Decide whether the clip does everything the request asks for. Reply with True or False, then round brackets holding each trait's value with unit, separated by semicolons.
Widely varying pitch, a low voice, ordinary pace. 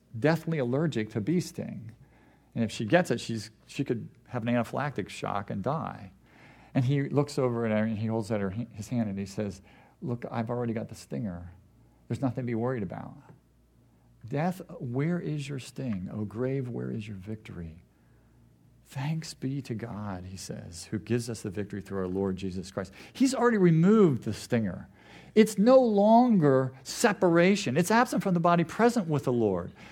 True (6.9 semitones; 120 Hz; 185 wpm)